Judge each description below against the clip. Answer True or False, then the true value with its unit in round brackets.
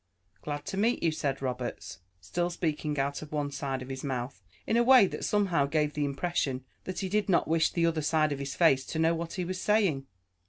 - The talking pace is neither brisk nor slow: False (230 wpm)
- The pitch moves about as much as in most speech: True (4.2 semitones)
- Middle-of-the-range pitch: True (155 Hz)